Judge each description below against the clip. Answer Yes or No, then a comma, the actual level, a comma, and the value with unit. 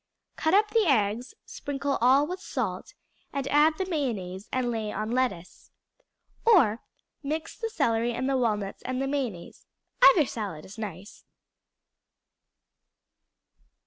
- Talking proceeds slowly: Yes, slow, 125 wpm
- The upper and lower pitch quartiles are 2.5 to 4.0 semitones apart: No, wide, 5.6 semitones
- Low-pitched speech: No, very high, 255 Hz